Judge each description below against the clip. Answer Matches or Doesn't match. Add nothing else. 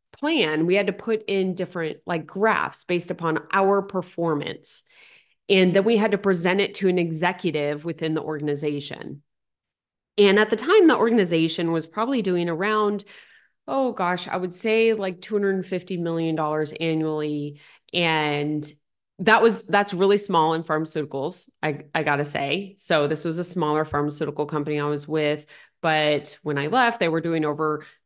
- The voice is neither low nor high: Matches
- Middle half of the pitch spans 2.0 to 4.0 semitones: Doesn't match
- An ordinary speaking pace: Matches